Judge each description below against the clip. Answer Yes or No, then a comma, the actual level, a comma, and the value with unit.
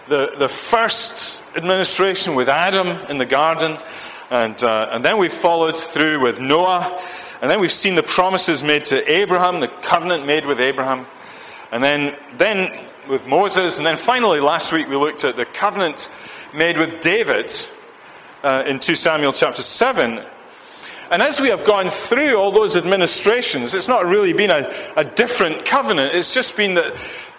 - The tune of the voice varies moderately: No, wide, 6.2 semitones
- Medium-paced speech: Yes, average, 170 wpm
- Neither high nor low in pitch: Yes, medium, 175 Hz